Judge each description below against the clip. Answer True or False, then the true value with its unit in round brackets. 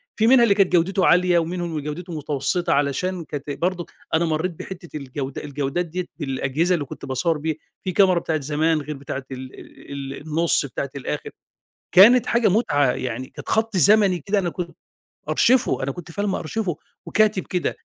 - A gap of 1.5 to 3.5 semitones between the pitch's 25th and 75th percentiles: False (4.3 semitones)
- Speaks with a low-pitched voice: False (170 Hz)